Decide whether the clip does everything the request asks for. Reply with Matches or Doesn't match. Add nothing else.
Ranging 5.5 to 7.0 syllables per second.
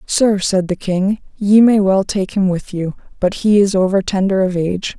Doesn't match